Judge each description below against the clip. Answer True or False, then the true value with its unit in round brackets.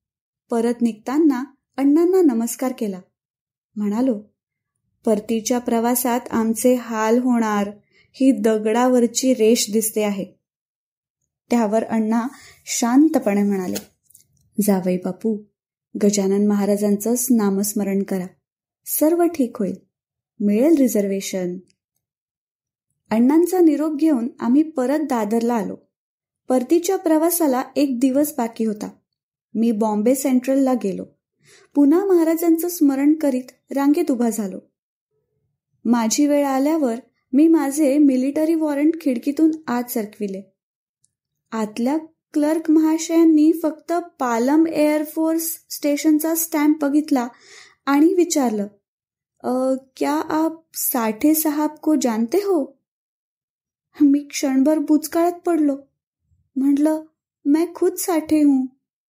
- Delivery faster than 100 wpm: False (90 wpm)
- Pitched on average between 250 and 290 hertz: True (265 Hz)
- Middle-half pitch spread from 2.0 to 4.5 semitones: False (5.5 semitones)